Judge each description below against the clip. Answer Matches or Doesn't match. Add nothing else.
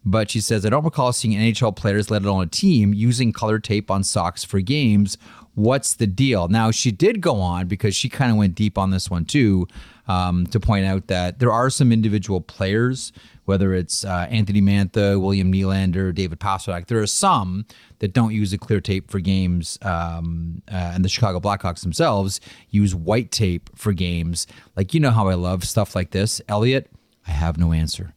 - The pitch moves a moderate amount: Matches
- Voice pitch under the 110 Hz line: Matches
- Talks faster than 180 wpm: Matches